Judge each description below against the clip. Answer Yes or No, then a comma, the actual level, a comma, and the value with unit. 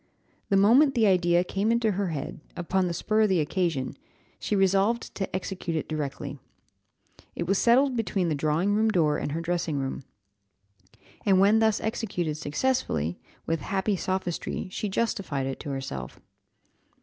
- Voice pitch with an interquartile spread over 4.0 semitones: Yes, average, 5.1 semitones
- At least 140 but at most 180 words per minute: Yes, average, 160 wpm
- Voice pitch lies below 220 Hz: Yes, medium, 185 Hz